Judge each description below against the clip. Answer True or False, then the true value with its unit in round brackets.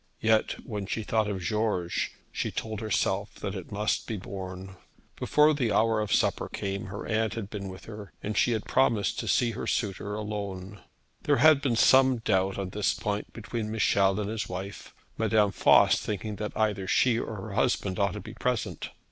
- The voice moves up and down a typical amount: False (2.3 semitones)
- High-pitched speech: False (105 Hz)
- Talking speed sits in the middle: True (190 wpm)